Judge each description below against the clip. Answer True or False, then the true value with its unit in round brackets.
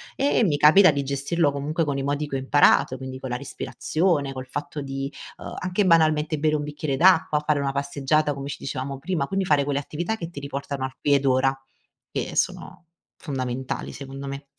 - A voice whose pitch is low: False (145 Hz)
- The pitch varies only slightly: True (2.2 semitones)